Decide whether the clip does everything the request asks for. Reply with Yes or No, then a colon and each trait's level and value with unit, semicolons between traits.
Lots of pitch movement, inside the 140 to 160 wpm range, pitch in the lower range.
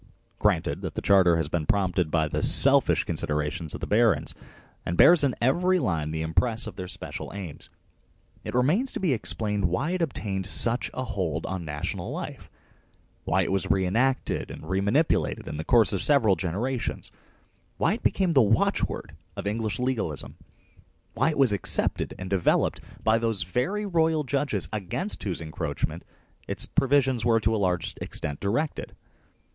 No: wide, 6.5 semitones; average, 170 wpm; low, 105 Hz